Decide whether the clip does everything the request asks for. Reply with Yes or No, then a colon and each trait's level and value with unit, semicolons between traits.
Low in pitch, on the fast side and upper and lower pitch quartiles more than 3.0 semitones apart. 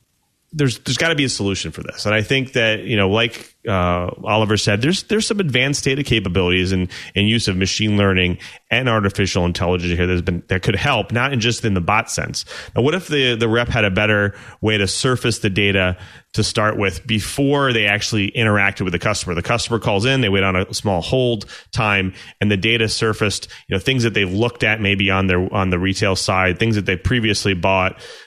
Yes: low, 105 Hz; fast, 225 wpm; average, 3.6 semitones